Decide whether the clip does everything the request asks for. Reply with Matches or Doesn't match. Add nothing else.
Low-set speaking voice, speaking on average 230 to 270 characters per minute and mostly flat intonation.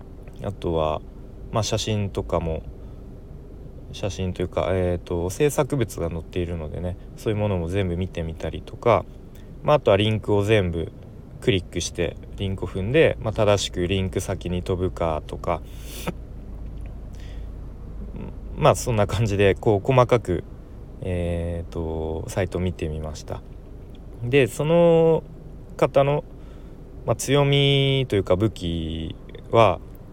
Doesn't match